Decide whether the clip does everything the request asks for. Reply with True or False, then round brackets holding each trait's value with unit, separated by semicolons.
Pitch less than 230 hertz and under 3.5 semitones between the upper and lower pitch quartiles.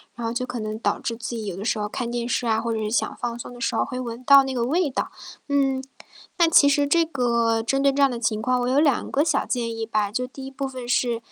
False (245 Hz; 2.9 semitones)